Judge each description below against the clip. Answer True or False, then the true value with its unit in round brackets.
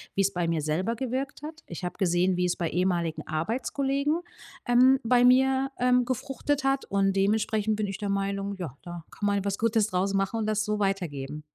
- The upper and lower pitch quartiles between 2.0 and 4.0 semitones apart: False (5.6 semitones)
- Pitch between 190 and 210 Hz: True (200 Hz)